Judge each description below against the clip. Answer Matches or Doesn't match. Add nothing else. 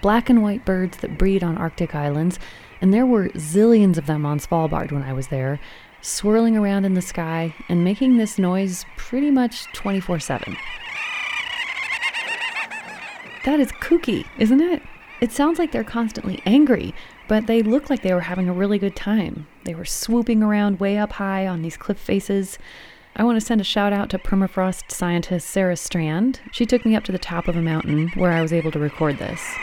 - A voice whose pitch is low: Doesn't match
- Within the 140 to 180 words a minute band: Doesn't match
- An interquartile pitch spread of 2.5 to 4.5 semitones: Doesn't match